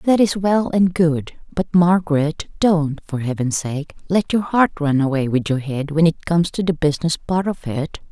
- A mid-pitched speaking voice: Yes, medium, 160 Hz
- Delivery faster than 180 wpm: Yes, fast, 205 wpm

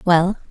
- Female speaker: Yes, female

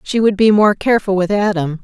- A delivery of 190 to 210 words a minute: No, fast, 230 wpm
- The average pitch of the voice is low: No, high, 200 Hz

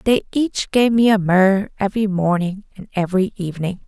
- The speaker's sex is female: Yes, female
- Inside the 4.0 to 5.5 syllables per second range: Yes, 5.2 syllables/s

